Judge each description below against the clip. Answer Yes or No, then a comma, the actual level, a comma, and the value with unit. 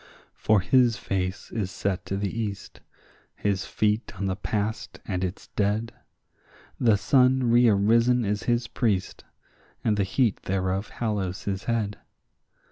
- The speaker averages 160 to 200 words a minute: No, slow, 135 wpm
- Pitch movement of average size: Yes, average, 3.1 semitones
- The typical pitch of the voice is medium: No, low, 105 Hz